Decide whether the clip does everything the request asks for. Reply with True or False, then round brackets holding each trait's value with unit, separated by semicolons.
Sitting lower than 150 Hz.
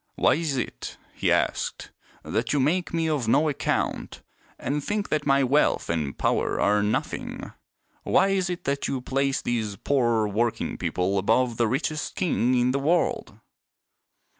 True (135 Hz)